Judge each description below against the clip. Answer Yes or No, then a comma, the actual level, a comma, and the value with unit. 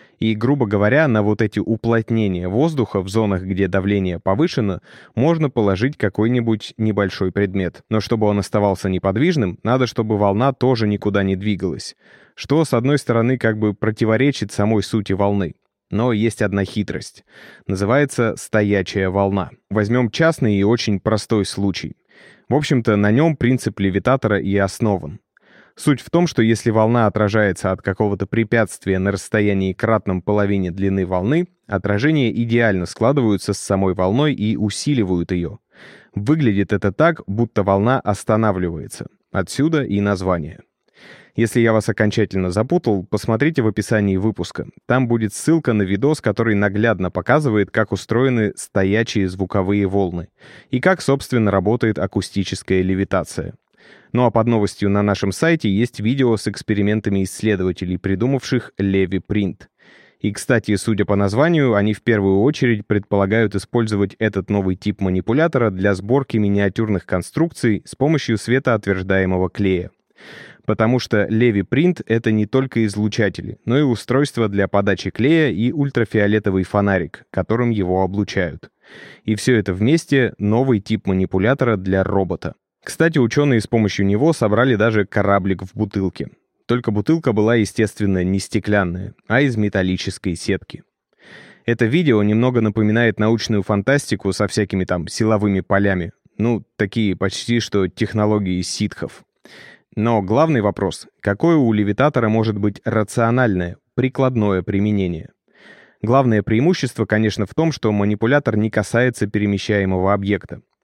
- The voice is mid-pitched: No, low, 105 Hz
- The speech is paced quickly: No, average, 135 wpm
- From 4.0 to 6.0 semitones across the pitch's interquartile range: No, average, 3.1 semitones